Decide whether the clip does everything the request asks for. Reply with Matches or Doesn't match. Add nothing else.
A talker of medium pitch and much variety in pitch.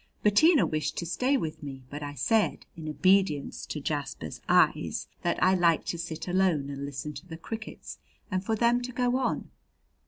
Matches